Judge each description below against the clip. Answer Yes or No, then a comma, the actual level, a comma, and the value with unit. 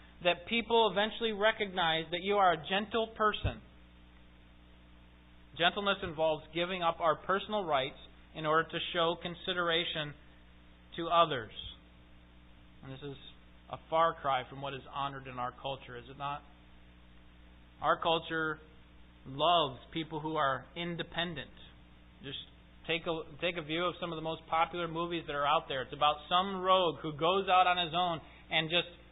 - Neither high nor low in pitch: Yes, medium, 160 Hz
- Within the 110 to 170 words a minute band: Yes, average, 155 wpm